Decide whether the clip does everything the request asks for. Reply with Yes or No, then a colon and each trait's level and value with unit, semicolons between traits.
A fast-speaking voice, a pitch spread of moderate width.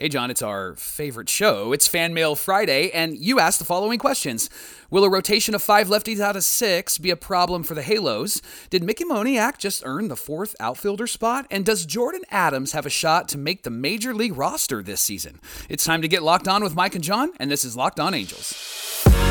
No: fast, 220 wpm; wide, 5.9 semitones